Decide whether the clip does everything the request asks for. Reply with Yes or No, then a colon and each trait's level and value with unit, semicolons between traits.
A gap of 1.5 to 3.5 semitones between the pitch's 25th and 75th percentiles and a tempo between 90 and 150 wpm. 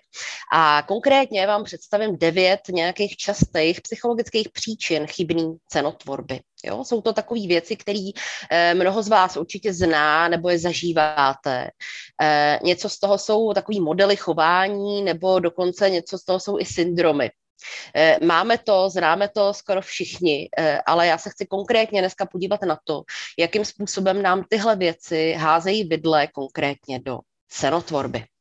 No: average, 4.1 semitones; average, 135 wpm